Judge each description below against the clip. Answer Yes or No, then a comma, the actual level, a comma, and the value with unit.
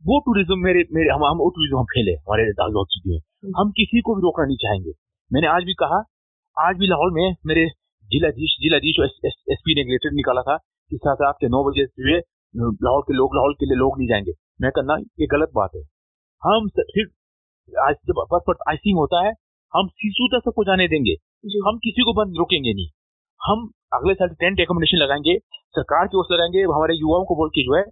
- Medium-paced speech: No, fast, 205 wpm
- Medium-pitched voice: Yes, medium, 165 Hz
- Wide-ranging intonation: Yes, wide, 6.0 semitones